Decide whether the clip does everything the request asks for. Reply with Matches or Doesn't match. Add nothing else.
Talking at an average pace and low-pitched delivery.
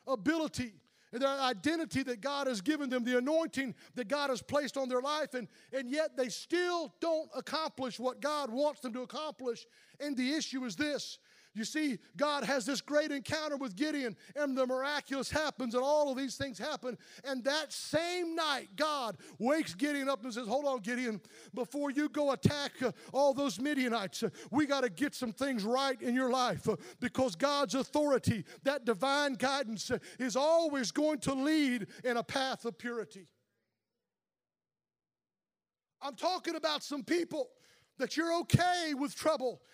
Doesn't match